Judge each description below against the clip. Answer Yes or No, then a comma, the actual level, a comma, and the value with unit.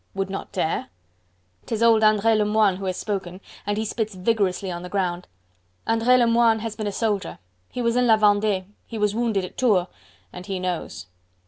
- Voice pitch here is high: Yes, high, 210 Hz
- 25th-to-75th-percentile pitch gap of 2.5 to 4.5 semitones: Yes, average, 3.1 semitones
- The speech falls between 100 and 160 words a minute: No, average, 190 wpm